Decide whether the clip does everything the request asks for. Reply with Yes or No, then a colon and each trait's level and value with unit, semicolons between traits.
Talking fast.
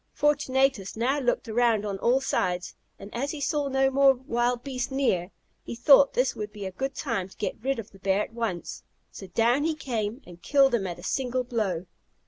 Yes: fast, 210 wpm